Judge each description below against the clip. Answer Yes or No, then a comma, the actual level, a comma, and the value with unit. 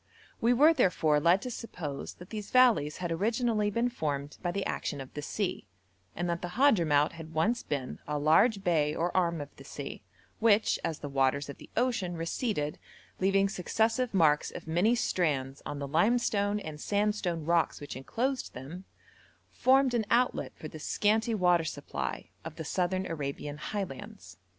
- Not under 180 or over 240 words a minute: No, average, 170 wpm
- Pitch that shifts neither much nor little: No, wide, 6.4 semitones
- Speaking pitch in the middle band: Yes, medium, 175 Hz